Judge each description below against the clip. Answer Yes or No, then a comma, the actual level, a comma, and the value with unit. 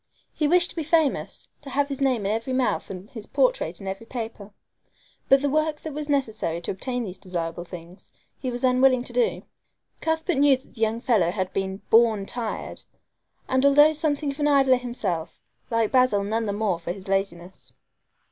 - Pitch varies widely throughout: Yes, wide, 6.2 semitones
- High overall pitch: Yes, high, 240 Hz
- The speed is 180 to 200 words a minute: Yes, average, 195 wpm